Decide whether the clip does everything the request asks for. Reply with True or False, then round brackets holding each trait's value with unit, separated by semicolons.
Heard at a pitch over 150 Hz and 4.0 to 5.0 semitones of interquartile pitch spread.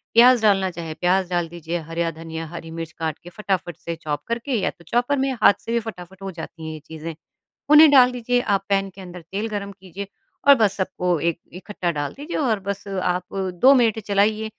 True (190 Hz; 4.4 semitones)